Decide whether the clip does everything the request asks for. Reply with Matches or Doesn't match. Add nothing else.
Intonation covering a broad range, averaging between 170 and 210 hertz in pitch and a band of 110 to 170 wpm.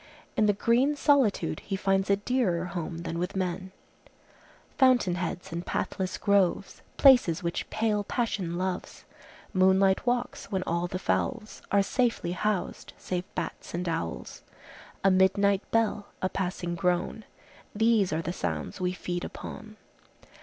Doesn't match